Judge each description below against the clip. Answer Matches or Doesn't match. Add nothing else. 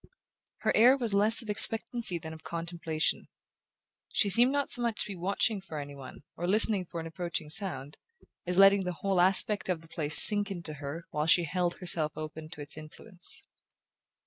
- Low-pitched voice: Doesn't match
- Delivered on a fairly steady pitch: Doesn't match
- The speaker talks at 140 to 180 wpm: Doesn't match